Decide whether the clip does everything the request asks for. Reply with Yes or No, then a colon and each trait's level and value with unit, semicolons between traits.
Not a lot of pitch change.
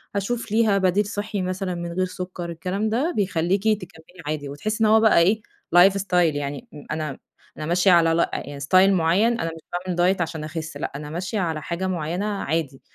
No: average, 3.5 semitones